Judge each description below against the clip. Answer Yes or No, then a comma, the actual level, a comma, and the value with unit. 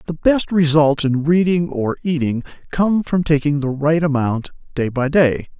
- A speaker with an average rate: Yes, average, 170 wpm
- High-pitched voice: No, medium, 155 Hz